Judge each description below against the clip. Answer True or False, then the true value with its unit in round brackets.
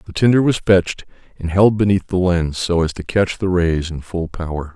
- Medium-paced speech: False (225 wpm)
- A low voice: True (90 Hz)